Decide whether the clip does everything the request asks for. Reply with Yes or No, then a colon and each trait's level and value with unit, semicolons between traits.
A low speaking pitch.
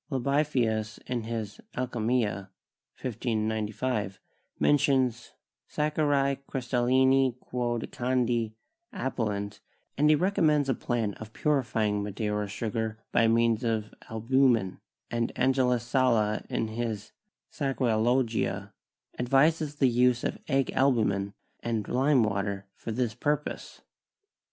Yes: low, 120 Hz